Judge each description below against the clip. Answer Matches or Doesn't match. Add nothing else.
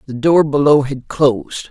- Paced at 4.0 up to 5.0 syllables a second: Matches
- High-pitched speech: Doesn't match